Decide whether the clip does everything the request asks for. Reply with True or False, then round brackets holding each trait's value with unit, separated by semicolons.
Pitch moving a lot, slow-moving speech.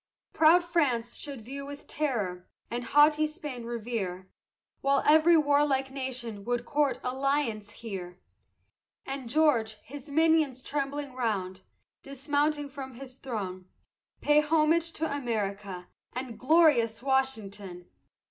False (4.5 semitones; 115 wpm)